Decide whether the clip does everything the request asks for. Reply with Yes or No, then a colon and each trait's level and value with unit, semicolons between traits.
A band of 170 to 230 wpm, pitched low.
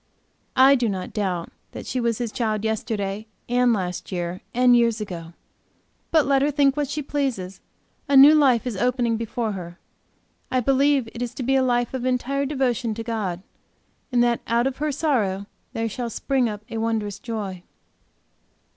No: average, 180 wpm; high, 235 Hz